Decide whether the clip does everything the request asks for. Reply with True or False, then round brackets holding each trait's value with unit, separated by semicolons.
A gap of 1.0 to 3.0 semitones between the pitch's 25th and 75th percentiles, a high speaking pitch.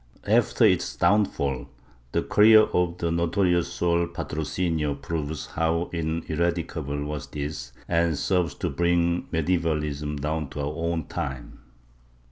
False (2.7 semitones; 80 Hz)